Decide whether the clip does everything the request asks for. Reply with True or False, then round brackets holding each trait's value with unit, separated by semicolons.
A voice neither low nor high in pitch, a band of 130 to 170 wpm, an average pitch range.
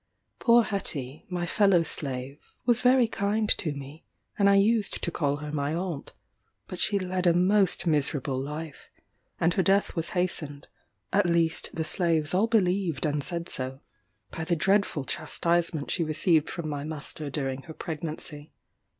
True (165 Hz; 160 wpm; 4.3 semitones)